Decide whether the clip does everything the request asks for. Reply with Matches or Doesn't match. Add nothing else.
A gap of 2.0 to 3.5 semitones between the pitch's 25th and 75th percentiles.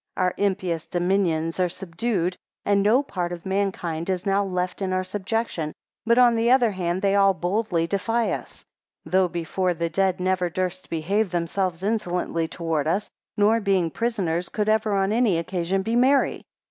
Matches